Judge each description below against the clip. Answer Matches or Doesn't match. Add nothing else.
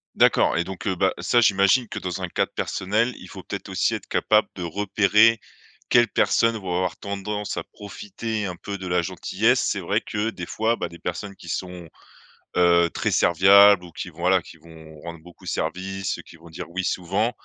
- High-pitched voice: Doesn't match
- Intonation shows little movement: Doesn't match